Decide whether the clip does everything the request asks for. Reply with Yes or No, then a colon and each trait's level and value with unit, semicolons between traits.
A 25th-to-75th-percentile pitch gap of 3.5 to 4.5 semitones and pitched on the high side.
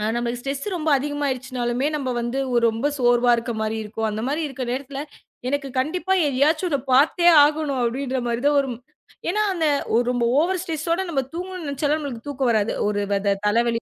Yes: average, 4.0 semitones; very high, 270 Hz